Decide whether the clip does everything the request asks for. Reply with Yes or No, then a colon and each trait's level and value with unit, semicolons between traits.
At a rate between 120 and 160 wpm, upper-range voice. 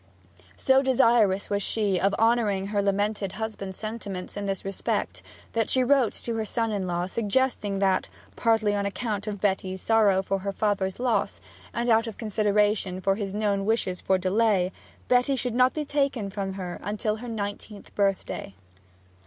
No: average, 170 wpm; high, 205 Hz